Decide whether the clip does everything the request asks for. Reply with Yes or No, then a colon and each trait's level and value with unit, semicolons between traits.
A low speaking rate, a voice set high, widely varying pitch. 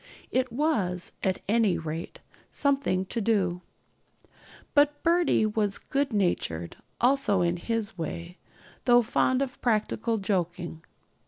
Yes: slow, 115 wpm; high, 215 Hz; wide, 6.1 semitones